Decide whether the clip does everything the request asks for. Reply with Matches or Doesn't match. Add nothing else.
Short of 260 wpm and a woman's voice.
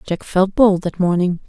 Matches